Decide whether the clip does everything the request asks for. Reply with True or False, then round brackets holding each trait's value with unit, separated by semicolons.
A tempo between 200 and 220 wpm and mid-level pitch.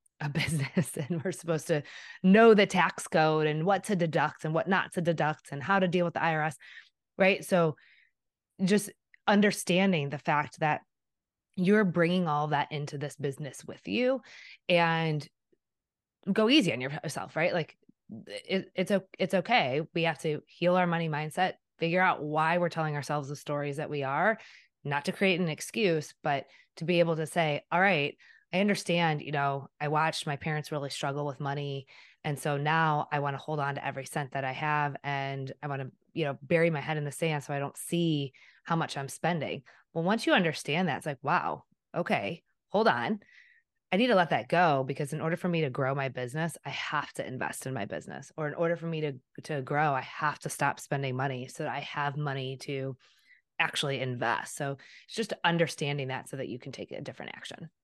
True (205 wpm; 155 Hz)